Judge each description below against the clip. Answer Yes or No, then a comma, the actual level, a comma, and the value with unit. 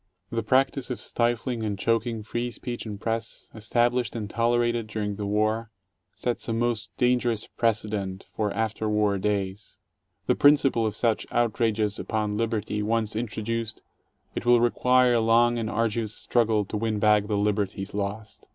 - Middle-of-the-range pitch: No, low, 110 Hz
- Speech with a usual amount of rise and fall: No, narrow, 2.1 semitones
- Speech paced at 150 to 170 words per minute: Yes, average, 155 wpm